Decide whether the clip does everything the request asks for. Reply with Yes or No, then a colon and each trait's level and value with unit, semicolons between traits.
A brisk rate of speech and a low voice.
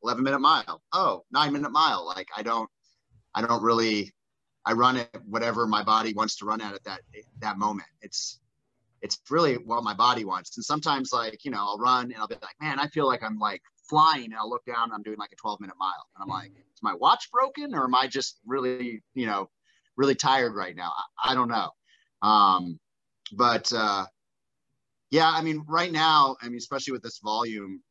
Yes: fast, 210 wpm; low, 120 Hz